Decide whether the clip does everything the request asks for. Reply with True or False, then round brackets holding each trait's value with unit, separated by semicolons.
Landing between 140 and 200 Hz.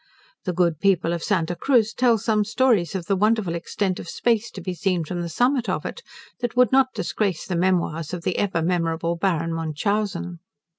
True (185 Hz)